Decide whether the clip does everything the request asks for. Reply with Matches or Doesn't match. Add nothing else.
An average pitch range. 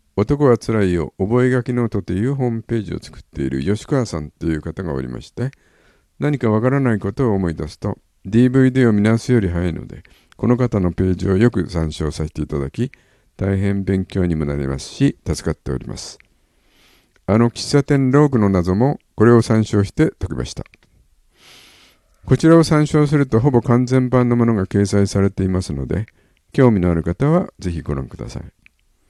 Doesn't match